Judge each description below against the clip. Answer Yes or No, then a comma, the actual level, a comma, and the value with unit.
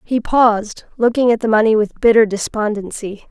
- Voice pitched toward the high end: Yes, high, 220 Hz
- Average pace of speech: Yes, average, 165 wpm